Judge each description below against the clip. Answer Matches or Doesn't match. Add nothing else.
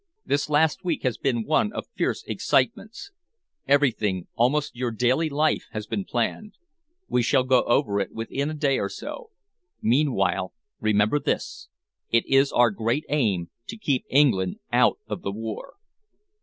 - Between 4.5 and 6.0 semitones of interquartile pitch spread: Matches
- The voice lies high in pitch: Doesn't match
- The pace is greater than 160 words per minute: Doesn't match